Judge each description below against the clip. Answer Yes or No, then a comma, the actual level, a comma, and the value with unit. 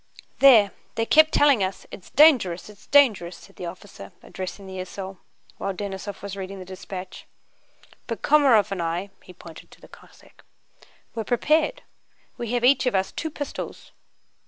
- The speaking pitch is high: Yes, high, 200 Hz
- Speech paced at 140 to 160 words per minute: Yes, average, 155 wpm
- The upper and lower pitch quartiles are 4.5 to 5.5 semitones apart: Yes, average, 5.1 semitones